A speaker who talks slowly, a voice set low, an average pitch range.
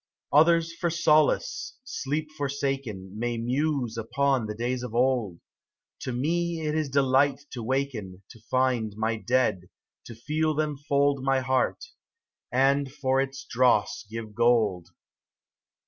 Yes: slow, 130 wpm; low, 130 Hz; average, 3.6 semitones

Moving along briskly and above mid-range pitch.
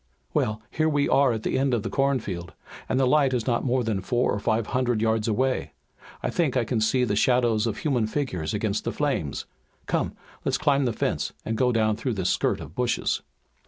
No: fast, 215 wpm; low, 120 Hz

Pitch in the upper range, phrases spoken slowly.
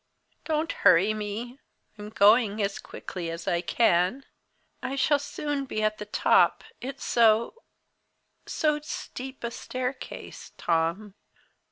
Yes: high, 220 Hz; slow, 125 wpm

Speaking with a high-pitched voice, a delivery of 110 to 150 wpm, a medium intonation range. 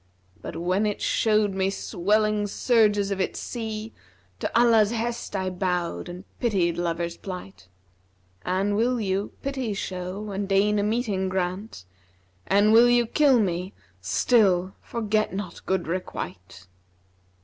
Yes: high, 195 Hz; average, 140 wpm; average, 3.3 semitones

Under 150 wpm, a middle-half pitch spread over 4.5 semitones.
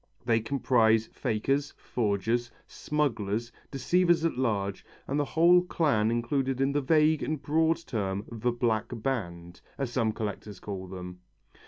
Yes: average, 140 wpm; average, 5.2 semitones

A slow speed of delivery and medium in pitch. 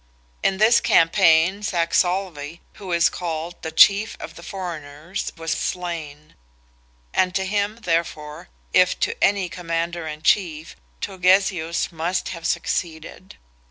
Yes: slow, 125 wpm; medium, 170 Hz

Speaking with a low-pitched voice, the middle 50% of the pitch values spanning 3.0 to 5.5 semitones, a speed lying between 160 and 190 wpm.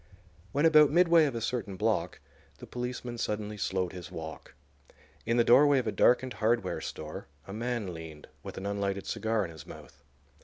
Yes: low, 110 Hz; average, 4.6 semitones; average, 180 wpm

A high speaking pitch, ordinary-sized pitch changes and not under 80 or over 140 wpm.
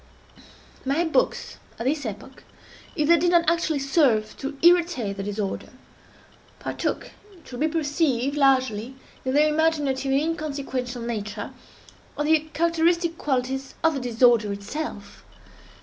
Yes: very high, 275 Hz; average, 4.6 semitones; slow, 135 wpm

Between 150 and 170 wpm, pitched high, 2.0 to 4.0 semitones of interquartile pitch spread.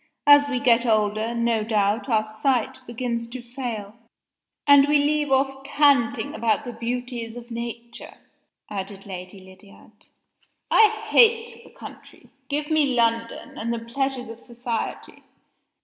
No: average, 140 wpm; high, 235 Hz; average, 3.3 semitones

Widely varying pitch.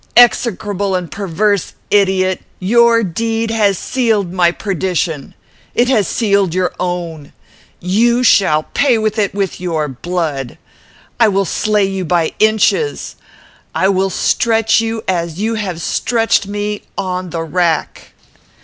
No: average, 3.8 semitones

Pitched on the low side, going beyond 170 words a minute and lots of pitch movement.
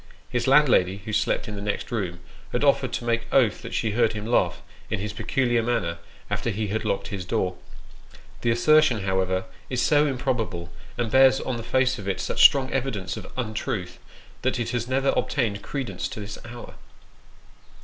No: low, 115 Hz; average, 190 wpm; average, 4.3 semitones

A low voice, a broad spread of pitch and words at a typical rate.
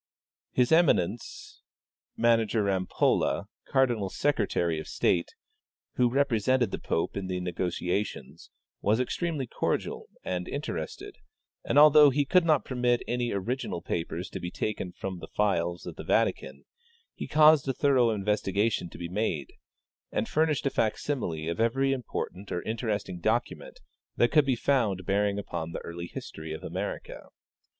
Yes: low, 110 Hz; wide, 6.4 semitones; average, 150 wpm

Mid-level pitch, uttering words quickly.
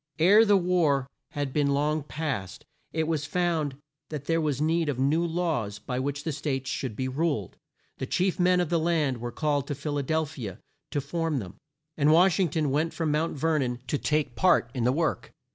Yes: medium, 150 Hz; fast, 215 wpm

